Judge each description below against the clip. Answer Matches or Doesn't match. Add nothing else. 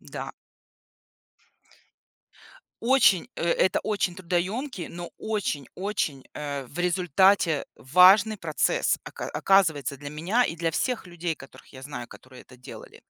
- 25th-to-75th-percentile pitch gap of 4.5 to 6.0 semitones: Matches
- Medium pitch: Matches